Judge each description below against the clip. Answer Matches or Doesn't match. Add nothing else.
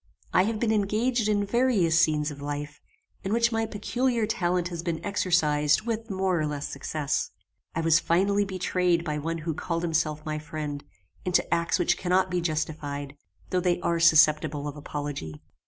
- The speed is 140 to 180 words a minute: Matches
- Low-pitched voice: Doesn't match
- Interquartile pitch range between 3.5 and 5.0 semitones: Matches